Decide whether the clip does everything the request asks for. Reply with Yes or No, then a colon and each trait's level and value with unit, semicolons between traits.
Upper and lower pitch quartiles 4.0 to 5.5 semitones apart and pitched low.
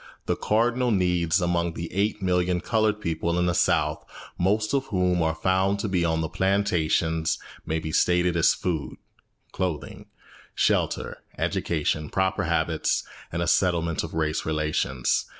No: average, 2.9 semitones; very low, 90 Hz